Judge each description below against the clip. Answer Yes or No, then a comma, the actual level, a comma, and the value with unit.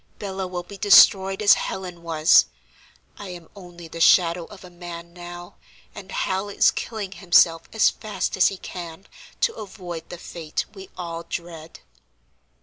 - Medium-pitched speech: Yes, medium, 180 Hz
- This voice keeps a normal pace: Yes, average, 155 wpm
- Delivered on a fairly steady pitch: Yes, narrow, 2.2 semitones